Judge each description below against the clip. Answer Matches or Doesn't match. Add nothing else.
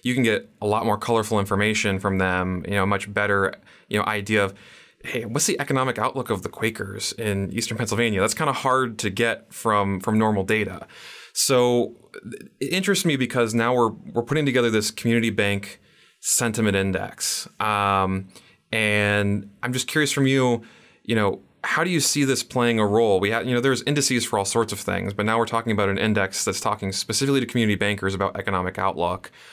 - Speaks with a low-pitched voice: Matches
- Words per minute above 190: Matches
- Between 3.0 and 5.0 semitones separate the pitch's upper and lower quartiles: Matches